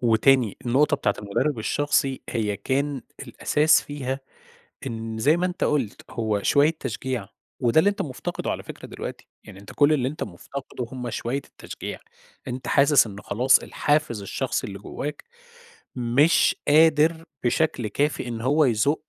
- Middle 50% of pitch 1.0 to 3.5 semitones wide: No, average, 4.2 semitones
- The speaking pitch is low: Yes, low, 130 Hz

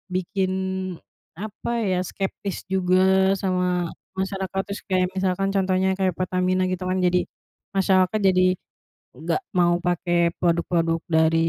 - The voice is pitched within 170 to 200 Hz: Yes, medium, 185 Hz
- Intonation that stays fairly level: Yes, narrow, 1.2 semitones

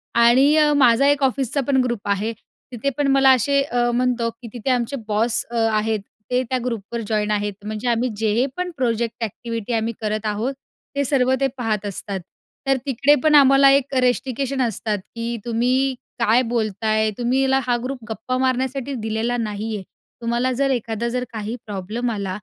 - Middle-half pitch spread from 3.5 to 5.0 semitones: No, average, 3.1 semitones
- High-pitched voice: Yes, high, 240 Hz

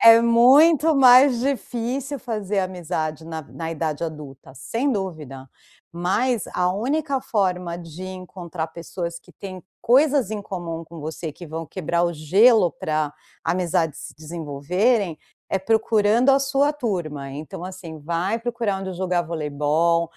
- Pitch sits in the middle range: Yes, medium, 180 Hz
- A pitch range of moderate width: No, wide, 6.1 semitones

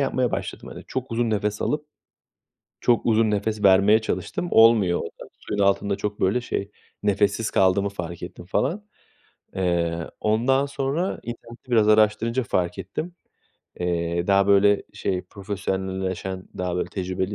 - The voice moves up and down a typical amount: Yes, average, 3.5 semitones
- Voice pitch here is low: Yes, low, 100 Hz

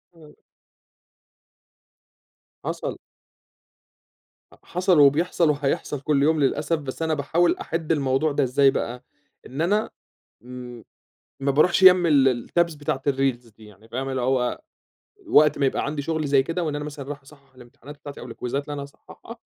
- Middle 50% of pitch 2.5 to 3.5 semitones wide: Yes, average, 2.8 semitones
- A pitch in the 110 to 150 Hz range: Yes, medium, 140 Hz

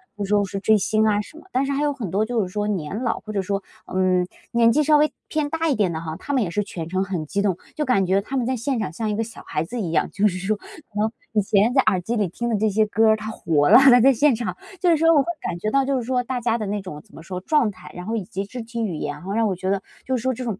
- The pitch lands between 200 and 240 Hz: Yes, high, 215 Hz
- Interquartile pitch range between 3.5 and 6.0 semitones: Yes, average, 4.6 semitones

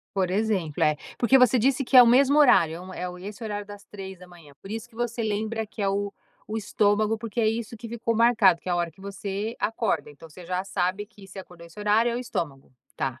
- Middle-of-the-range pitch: No, high, 205 Hz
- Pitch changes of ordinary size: Yes, average, 3.9 semitones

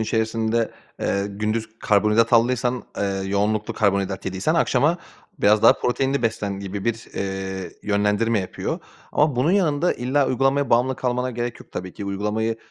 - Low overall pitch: Yes, low, 110 Hz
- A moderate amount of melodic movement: Yes, average, 3.7 semitones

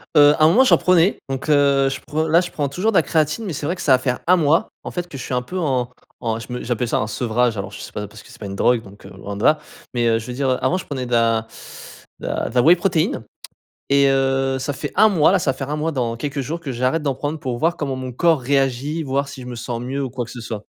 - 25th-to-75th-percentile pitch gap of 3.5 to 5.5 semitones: Yes, average, 4.1 semitones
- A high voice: No, low, 135 Hz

